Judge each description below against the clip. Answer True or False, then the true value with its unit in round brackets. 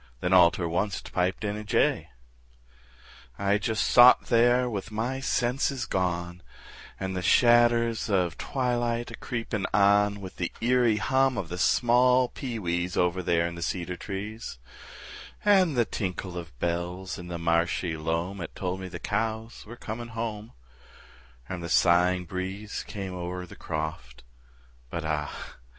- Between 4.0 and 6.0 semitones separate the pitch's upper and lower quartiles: True (5.0 semitones)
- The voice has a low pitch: True (95 Hz)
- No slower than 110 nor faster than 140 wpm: False (155 wpm)